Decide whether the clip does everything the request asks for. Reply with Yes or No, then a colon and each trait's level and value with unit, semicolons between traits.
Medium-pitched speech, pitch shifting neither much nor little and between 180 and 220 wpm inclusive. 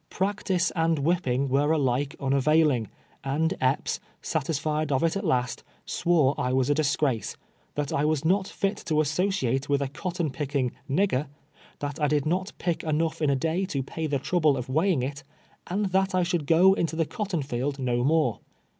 Yes: medium, 150 Hz; average, 3.9 semitones; average, 190 wpm